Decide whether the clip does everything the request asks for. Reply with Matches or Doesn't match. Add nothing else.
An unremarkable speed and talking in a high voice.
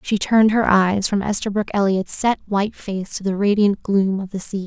Doesn't match